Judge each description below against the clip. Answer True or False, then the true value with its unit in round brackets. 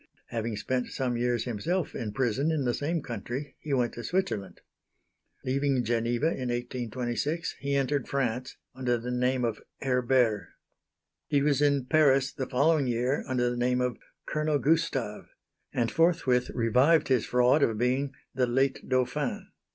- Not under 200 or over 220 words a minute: False (150 wpm)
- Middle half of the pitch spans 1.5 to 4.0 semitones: True (2.6 semitones)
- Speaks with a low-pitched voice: True (130 Hz)